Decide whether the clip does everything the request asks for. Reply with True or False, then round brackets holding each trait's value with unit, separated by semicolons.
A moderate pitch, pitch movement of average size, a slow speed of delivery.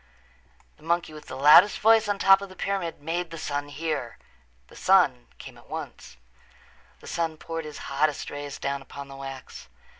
False (155 Hz; 3.9 semitones; 180 wpm)